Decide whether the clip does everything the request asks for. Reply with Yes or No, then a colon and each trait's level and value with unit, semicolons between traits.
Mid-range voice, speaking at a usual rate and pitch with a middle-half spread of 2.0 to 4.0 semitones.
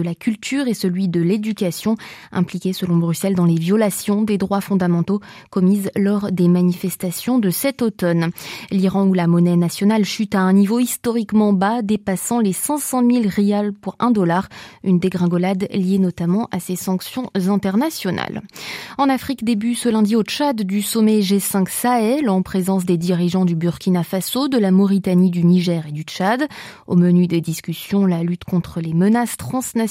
No: high, 195 Hz; average, 175 wpm; average, 3.3 semitones